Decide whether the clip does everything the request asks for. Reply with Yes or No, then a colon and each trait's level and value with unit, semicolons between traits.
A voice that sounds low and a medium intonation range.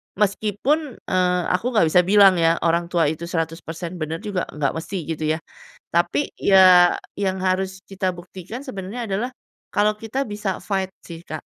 No: medium, 185 Hz; average, 3.3 semitones